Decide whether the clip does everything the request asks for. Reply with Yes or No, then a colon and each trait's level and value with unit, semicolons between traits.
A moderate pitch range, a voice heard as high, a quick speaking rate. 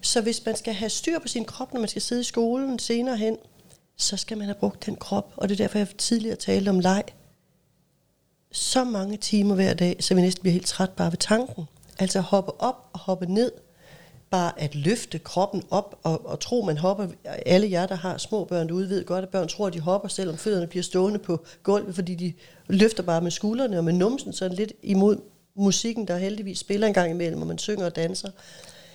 Yes: average, 3.2 semitones; high, 195 Hz; fast, 230 wpm